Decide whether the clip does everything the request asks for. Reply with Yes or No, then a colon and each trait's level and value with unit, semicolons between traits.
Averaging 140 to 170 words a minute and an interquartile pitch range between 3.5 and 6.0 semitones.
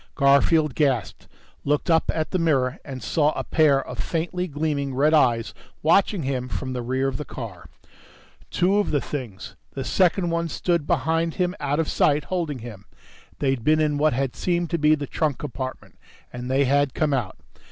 No: average, 185 wpm; average, 3.8 semitones